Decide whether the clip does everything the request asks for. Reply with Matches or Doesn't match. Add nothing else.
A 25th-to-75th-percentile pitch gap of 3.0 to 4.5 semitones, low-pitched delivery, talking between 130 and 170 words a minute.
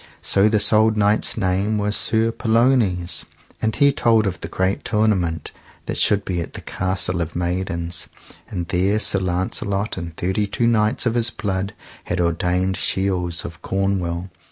Matches